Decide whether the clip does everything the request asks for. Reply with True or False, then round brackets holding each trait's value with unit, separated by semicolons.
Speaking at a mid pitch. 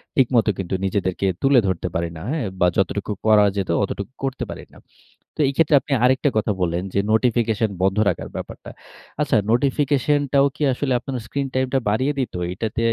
False (120 Hz)